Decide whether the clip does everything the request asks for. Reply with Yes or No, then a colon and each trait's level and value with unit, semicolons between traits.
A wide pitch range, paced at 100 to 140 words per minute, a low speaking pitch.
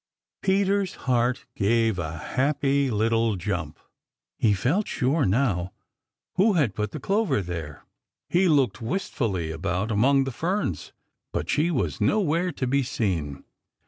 Yes: wide, 7.7 semitones; slow, 135 wpm; low, 125 Hz